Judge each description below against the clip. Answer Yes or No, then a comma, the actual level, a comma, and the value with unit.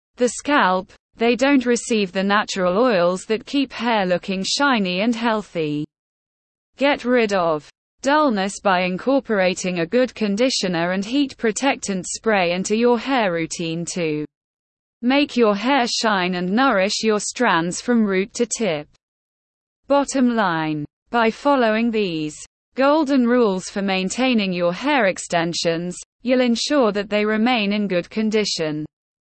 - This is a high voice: Yes, high, 215 Hz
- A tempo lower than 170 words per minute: Yes, slow, 135 wpm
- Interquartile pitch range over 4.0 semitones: Yes, wide, 5.4 semitones